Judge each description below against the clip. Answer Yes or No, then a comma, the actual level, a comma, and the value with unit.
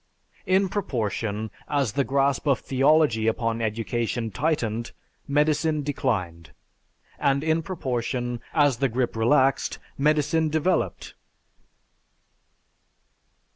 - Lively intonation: No, average, 4.8 semitones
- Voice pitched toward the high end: No, low, 135 Hz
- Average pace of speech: No, slow, 95 wpm